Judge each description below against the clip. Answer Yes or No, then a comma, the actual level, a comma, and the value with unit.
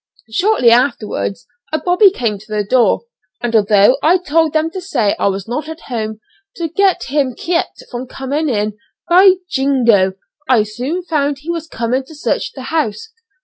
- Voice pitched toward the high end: Yes, very high, 265 Hz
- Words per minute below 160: No, average, 175 wpm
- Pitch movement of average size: No, wide, 6.7 semitones